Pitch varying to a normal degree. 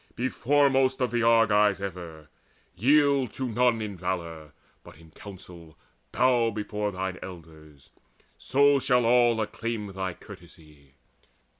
No: wide, 5.9 semitones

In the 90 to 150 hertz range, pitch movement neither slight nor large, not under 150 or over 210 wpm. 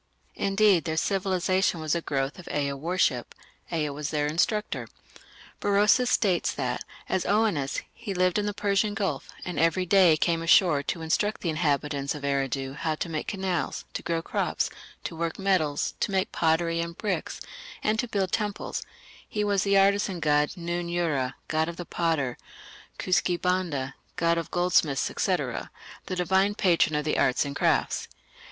No: medium, 170 Hz; average, 4.1 semitones; average, 165 wpm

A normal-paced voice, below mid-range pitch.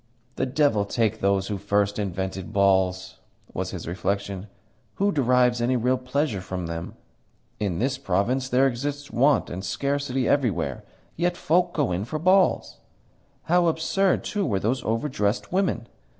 Yes: average, 150 wpm; low, 120 Hz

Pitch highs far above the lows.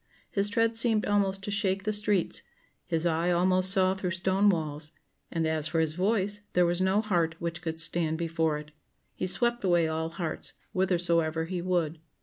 No: average, 3.1 semitones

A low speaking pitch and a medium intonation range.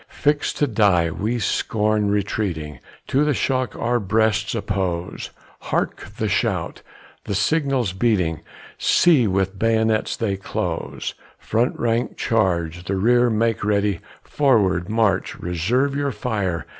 Yes: low, 105 Hz; average, 4.0 semitones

